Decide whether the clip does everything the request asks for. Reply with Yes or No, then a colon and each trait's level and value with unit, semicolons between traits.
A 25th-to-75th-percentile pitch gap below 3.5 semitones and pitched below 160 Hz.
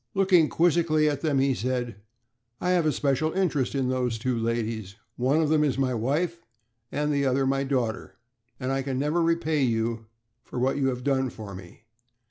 No: average, 3.8 semitones; low, 135 Hz